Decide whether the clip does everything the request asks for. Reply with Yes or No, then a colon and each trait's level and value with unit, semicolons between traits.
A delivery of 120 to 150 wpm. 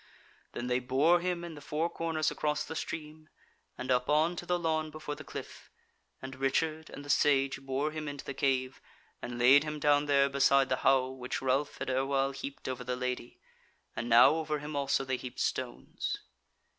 No: average, 195 wpm